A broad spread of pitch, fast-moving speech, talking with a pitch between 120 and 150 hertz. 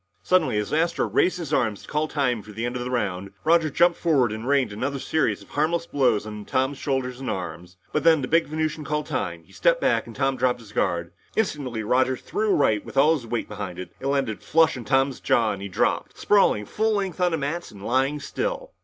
Yes: wide, 6.5 semitones; fast, 240 wpm; low, 135 Hz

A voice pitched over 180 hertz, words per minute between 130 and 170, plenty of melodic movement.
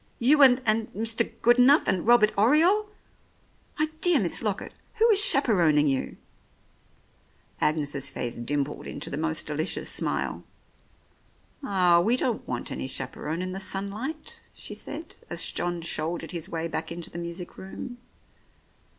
Yes: high, 190 Hz; average, 150 wpm; wide, 7.0 semitones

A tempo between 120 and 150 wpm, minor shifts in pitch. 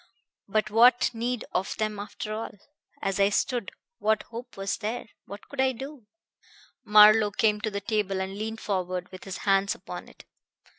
No: average, 170 wpm; narrow, 2.3 semitones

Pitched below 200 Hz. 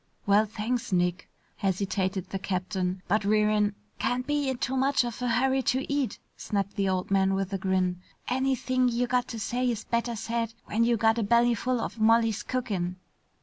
No: high, 225 Hz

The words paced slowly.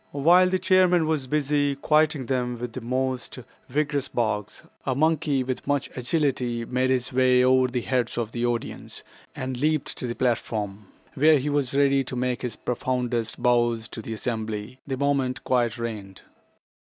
No: average, 165 wpm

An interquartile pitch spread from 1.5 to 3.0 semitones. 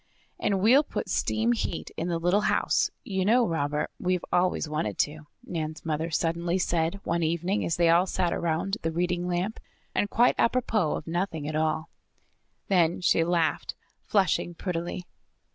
Yes: average, 2.7 semitones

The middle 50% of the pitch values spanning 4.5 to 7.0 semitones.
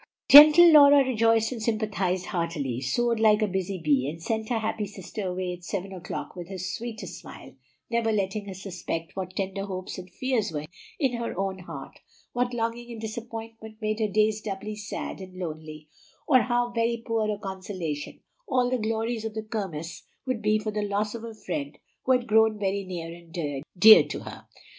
No: average, 3.7 semitones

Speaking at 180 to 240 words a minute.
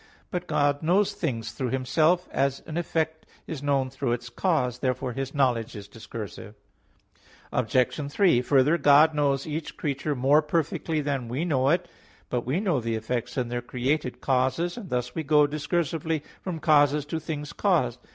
No: average, 170 wpm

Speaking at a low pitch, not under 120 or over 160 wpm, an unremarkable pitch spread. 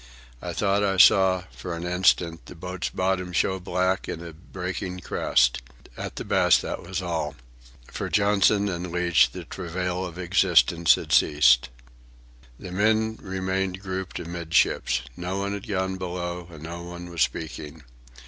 No: very low, 90 Hz; average, 155 wpm; narrow, 1.8 semitones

